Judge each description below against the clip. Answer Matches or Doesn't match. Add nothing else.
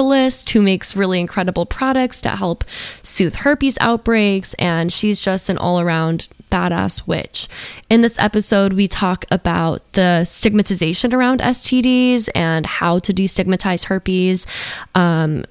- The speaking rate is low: Matches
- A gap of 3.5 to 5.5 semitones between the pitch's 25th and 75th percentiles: Matches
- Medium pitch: Doesn't match